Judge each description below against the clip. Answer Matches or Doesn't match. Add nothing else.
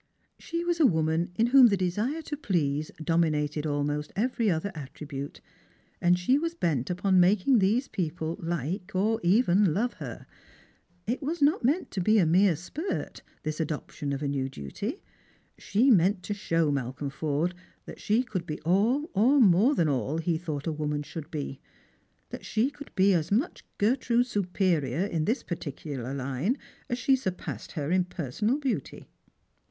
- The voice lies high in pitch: Doesn't match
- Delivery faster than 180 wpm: Doesn't match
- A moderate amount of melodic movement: Doesn't match